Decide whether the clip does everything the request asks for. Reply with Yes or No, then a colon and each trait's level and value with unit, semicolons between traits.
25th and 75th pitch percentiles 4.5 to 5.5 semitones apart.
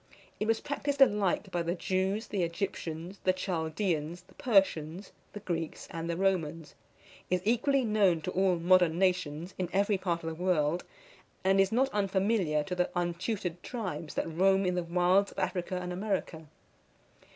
No: average, 2.7 semitones